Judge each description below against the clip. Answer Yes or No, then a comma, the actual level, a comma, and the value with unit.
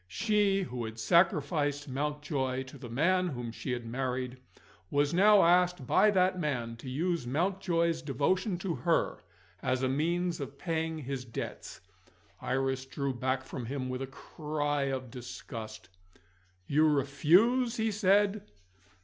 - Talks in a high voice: No, medium, 145 Hz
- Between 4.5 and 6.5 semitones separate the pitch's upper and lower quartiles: Yes, wide, 5.4 semitones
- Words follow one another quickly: No, average, 140 wpm